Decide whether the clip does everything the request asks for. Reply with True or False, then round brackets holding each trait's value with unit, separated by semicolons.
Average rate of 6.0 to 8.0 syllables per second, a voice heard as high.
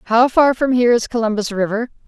True (6.3 syllables/s; 235 Hz)